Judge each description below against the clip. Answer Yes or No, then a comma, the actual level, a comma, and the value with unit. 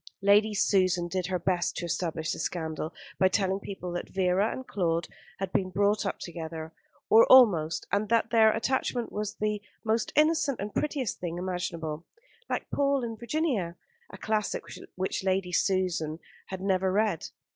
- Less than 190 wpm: Yes, average, 160 wpm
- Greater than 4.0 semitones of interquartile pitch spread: No, average, 3.7 semitones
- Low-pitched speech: No, high, 190 Hz